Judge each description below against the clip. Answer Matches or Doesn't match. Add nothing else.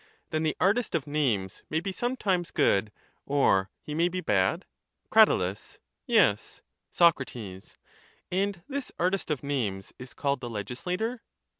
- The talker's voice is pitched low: Doesn't match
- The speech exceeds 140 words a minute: Doesn't match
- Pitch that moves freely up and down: Matches